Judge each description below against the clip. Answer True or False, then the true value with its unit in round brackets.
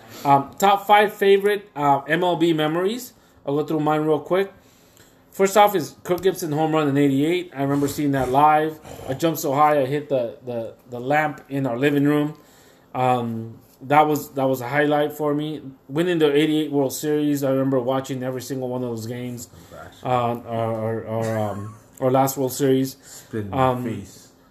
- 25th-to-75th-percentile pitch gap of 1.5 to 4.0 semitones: True (3.3 semitones)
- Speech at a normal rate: True (180 wpm)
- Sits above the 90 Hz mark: True (140 Hz)